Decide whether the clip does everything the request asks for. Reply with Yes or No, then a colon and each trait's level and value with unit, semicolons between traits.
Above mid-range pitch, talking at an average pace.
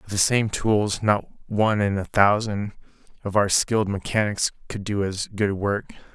No: low, 105 Hz; average, 175 wpm